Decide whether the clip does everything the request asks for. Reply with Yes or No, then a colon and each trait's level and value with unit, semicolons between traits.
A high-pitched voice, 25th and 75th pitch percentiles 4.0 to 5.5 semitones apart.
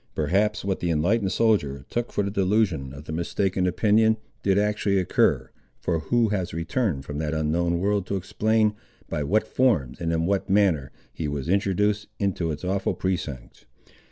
No: very low, 95 Hz; average, 4.5 semitones